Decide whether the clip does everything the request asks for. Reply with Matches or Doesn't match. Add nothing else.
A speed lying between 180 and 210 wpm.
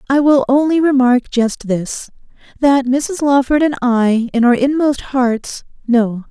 Doesn't match